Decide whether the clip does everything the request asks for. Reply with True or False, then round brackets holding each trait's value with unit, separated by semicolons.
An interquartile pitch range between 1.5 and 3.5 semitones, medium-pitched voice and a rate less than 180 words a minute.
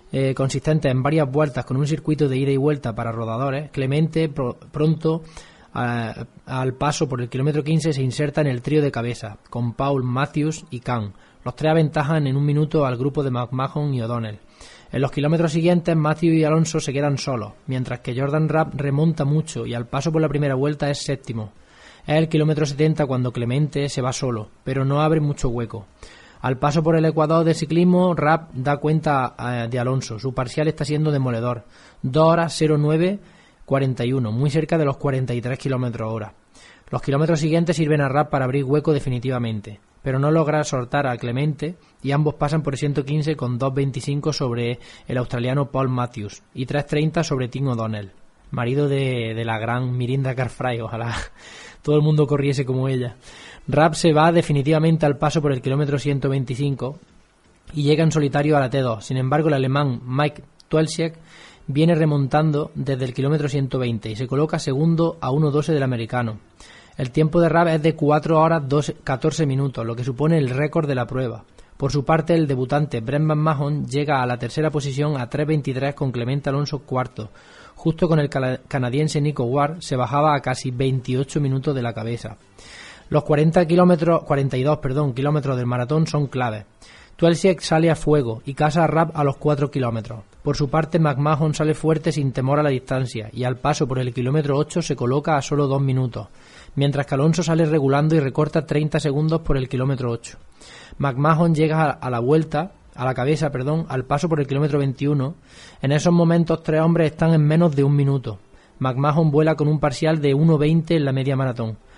False (3.2 semitones; 145 Hz; 185 wpm)